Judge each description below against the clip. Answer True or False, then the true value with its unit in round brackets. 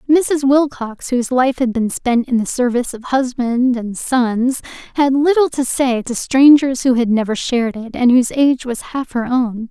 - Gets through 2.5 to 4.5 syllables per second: False (4.7 syllables/s)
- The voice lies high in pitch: True (255 Hz)